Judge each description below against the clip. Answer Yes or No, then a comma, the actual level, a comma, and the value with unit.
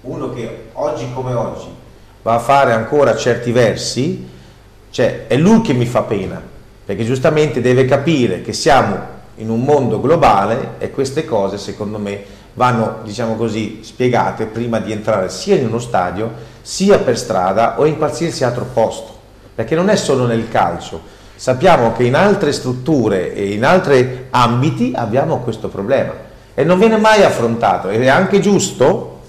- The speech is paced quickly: No, average, 160 wpm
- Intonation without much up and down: No, average, 4.2 semitones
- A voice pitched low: Yes, low, 120 Hz